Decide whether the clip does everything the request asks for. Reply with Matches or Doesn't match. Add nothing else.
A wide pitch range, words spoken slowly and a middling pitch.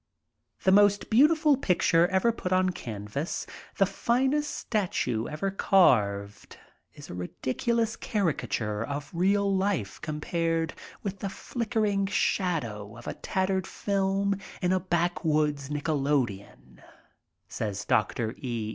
Matches